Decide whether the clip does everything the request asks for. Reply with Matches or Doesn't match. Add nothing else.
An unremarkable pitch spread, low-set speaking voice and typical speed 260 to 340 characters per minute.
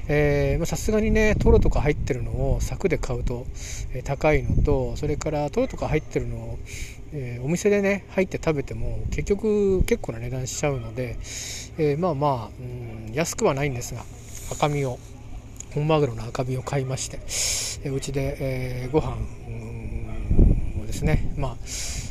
Matches